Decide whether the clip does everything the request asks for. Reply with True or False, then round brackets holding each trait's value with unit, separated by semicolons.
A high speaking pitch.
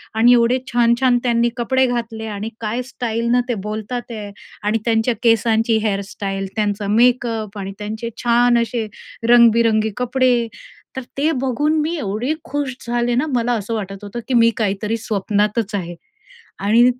True (230 Hz)